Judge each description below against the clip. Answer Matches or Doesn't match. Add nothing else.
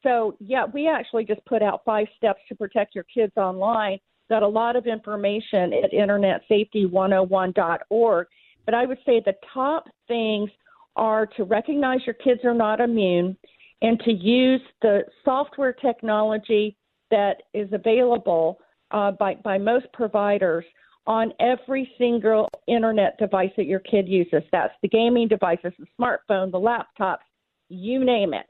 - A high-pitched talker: Matches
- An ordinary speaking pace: Matches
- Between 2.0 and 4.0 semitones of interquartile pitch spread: Matches